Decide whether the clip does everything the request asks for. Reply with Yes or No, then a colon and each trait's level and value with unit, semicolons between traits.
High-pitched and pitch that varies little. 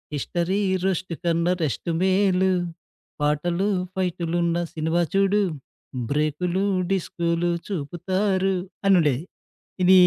No: medium, 175 Hz; narrow, 2.2 semitones